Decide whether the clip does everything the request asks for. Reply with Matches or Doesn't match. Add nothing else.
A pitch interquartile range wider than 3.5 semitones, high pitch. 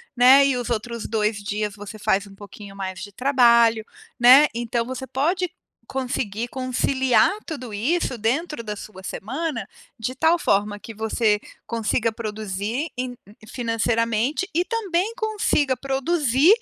Matches